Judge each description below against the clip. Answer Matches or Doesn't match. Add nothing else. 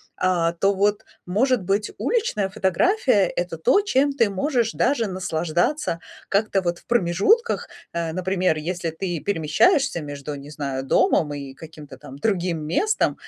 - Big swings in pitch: Matches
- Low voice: Doesn't match